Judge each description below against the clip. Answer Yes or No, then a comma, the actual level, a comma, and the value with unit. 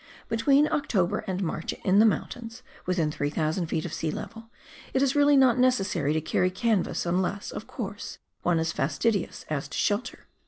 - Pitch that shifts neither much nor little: No, wide, 6.2 semitones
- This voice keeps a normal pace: Yes, average, 170 wpm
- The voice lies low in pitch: No, high, 190 Hz